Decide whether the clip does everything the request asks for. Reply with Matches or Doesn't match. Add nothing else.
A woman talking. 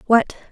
Matches